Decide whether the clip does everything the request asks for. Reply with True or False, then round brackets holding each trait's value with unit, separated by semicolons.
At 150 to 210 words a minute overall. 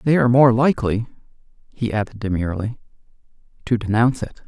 False (135 wpm)